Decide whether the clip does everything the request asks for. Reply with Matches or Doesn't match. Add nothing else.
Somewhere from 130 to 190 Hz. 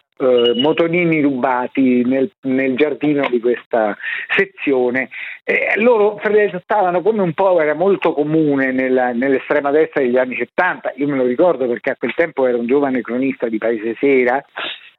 Matches